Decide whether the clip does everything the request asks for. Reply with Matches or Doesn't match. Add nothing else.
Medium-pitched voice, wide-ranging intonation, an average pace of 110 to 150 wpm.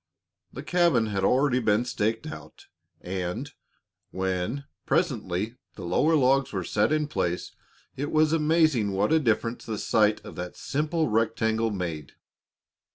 Doesn't match